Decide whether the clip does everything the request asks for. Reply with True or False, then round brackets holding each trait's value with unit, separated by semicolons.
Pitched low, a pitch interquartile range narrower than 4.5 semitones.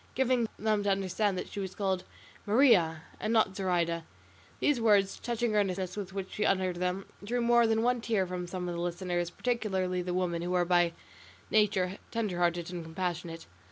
False (190 Hz; 3.3 semitones)